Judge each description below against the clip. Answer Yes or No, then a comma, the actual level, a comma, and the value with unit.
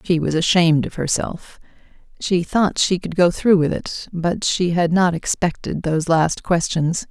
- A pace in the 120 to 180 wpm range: Yes, average, 175 wpm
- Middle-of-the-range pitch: Yes, medium, 170 Hz